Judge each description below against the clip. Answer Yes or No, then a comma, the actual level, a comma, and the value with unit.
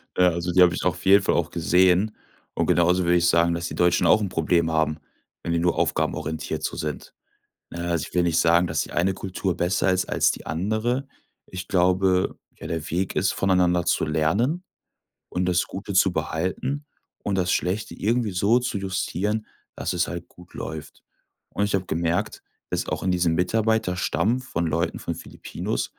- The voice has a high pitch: No, very low, 90 Hz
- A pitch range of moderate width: No, narrow, 2.3 semitones